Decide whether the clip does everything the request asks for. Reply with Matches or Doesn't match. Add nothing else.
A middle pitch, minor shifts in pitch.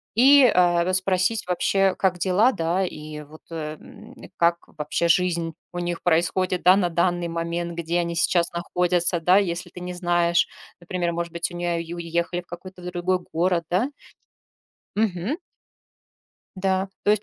Matches